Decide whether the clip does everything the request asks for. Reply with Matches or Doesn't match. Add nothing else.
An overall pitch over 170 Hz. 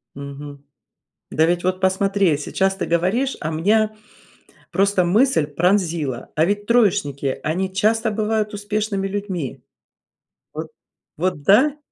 Matches